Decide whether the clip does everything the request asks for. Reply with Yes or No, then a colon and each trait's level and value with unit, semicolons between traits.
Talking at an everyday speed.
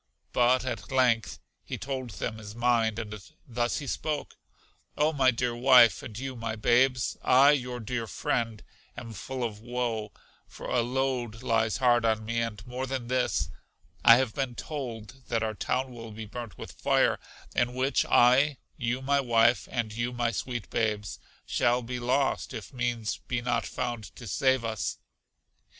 Yes: average, 170 wpm